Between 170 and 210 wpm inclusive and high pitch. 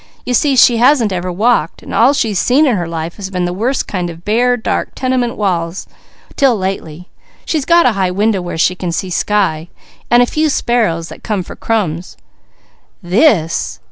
Yes: average, 190 wpm; high, 200 Hz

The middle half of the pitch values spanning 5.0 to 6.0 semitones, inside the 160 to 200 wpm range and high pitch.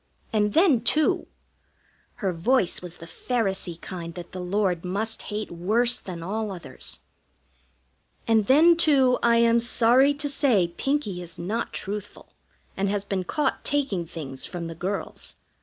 No: wide, 5.6 semitones; average, 150 wpm; high, 205 Hz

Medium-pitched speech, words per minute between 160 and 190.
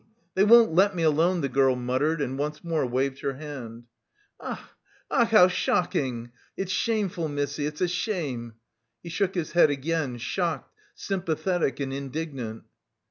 No: medium, 150 Hz; average, 150 wpm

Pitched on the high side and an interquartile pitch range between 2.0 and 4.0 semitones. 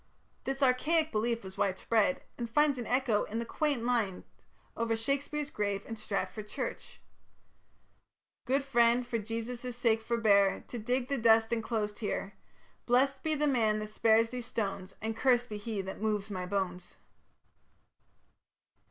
Yes: high, 230 Hz; average, 3.0 semitones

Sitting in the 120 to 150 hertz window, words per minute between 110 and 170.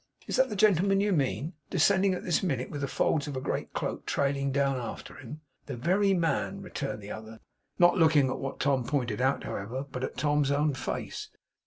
No: medium, 140 Hz; fast, 205 wpm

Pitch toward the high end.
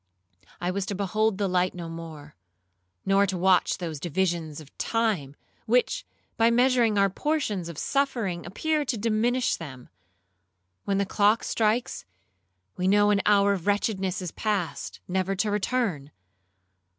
Yes: high, 200 Hz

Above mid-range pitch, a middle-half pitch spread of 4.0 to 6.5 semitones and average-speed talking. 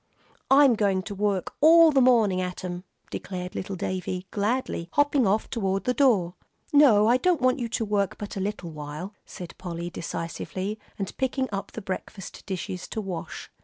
Yes: high, 200 Hz; average, 5.2 semitones; average, 175 wpm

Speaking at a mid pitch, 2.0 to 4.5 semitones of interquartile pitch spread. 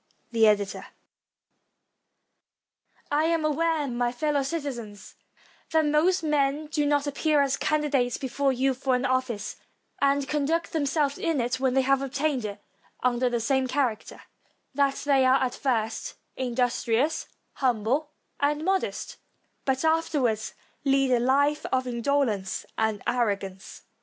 No: very high, 270 Hz; average, 3.2 semitones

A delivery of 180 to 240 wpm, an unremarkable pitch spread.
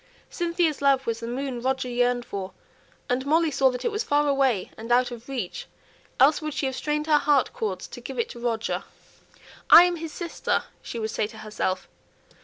Yes: fast, 205 wpm; average, 4.1 semitones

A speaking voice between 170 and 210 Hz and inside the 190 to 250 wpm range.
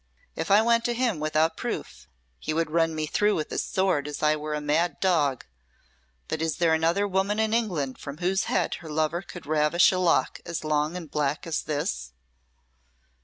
No: medium, 160 Hz; average, 195 wpm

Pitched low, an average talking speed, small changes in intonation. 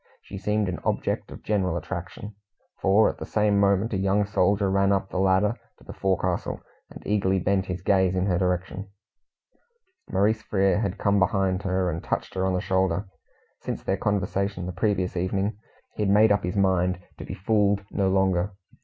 Yes: very low, 95 Hz; average, 190 wpm; narrow, 1.6 semitones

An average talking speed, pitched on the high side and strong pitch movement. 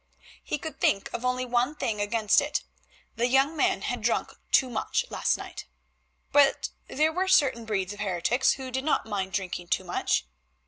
Yes: average, 180 wpm; very high, 250 Hz; wide, 5.7 semitones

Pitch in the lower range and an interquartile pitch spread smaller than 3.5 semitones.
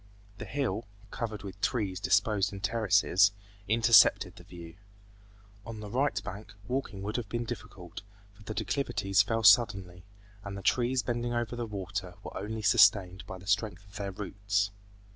Yes: low, 105 Hz; average, 2.8 semitones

